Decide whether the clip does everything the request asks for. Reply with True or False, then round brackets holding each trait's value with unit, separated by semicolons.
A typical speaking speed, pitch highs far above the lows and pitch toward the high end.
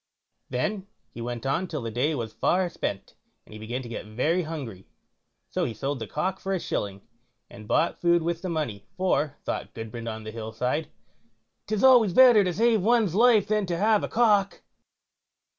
False (190 wpm; 8.9 semitones; 160 Hz)